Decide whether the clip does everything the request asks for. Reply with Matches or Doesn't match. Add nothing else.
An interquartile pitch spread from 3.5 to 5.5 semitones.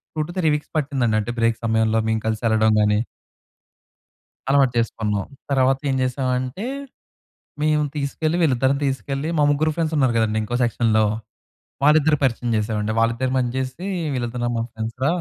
Matches